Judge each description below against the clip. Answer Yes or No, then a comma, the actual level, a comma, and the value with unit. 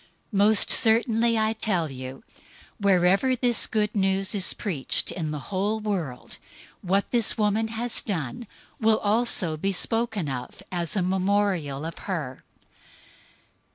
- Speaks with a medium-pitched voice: No, high, 200 Hz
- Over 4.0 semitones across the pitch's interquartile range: Yes, average, 4.4 semitones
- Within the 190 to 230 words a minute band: No, slow, 135 wpm